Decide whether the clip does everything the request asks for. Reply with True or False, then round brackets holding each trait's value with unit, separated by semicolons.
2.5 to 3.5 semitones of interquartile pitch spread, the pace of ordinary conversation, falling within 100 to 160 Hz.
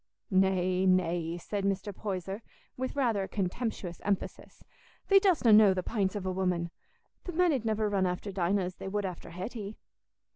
False (2.9 semitones; 175 wpm; 195 Hz)